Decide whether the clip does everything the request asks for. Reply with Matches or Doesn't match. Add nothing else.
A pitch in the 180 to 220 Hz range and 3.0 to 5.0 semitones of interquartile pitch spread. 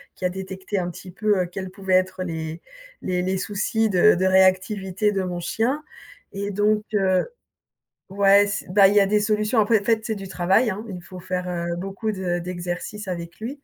Doesn't match